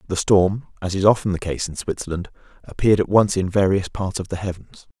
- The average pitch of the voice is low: Yes, very low, 95 Hz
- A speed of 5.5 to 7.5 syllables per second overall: Yes, 5.9 syllables/s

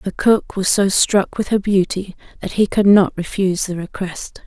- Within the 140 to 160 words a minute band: No, average, 200 wpm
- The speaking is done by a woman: Yes, female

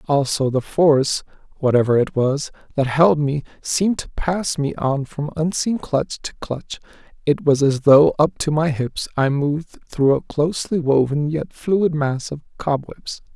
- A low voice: No, medium, 145 Hz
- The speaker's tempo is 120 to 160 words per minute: No, average, 170 wpm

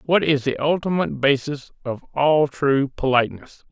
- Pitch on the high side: No, medium, 140 Hz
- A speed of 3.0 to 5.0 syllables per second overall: Yes, 4.9 syllables/s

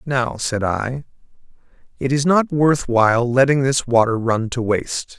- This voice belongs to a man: Yes, male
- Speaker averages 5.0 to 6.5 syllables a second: No, 4.3 syllables/s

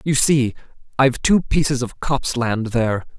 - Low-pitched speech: Yes, low, 130 Hz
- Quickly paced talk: No, average, 170 wpm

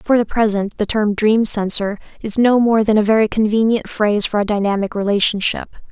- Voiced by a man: No, female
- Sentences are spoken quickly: No, average, 195 wpm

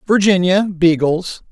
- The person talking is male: Yes, male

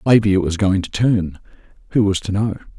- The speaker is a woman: No, male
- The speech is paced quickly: No, average, 195 wpm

